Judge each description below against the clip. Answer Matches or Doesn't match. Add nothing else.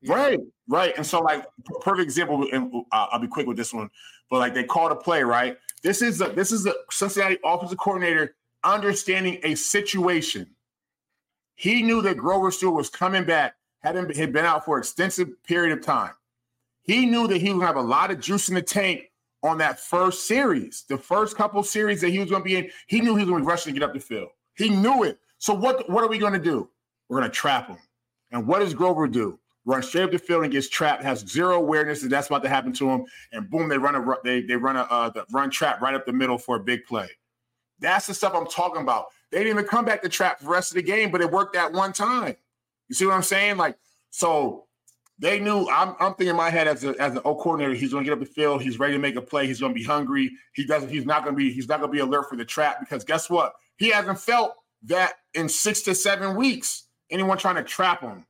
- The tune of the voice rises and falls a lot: Matches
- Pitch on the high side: Doesn't match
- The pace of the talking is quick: Matches